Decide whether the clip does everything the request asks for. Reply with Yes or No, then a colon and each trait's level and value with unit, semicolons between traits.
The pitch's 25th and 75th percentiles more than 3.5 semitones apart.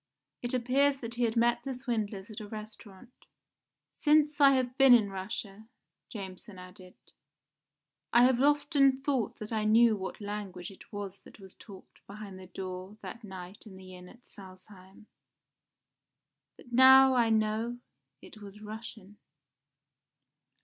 Yes: average, 4.1 semitones